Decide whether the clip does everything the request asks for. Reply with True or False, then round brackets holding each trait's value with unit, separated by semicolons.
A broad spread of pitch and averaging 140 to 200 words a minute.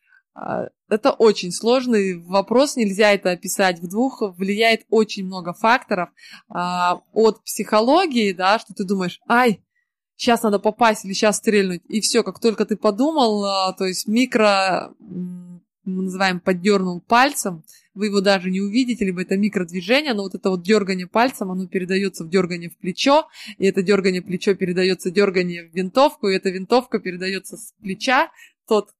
False (3.2 semitones; 155 wpm)